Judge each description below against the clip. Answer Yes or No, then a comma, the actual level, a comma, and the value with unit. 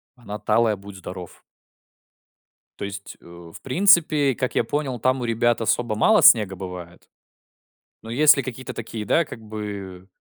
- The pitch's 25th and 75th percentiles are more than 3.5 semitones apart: Yes, average, 4.6 semitones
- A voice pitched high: No, low, 115 Hz